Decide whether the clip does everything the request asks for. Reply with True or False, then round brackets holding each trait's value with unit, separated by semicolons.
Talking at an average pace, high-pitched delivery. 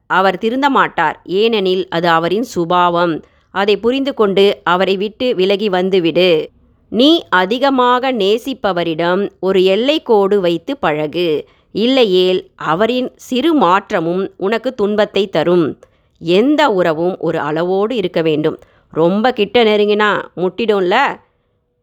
True (105 wpm; 195 Hz)